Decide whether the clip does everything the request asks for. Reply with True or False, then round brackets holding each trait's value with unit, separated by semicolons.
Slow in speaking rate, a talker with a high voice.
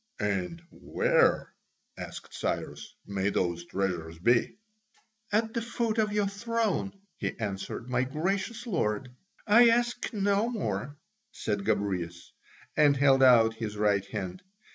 False (125 wpm; 130 Hz)